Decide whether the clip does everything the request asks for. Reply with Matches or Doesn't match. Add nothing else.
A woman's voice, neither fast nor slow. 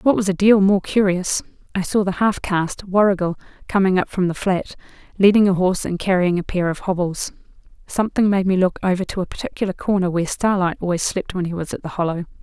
Doesn't match